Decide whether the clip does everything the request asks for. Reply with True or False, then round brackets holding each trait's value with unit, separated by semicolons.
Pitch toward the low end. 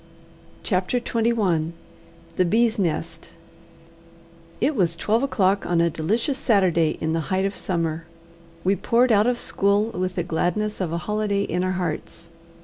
False (190 Hz)